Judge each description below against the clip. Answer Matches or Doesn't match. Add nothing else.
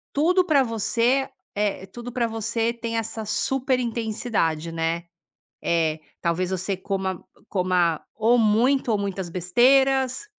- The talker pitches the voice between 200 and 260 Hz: Matches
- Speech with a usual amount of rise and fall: Matches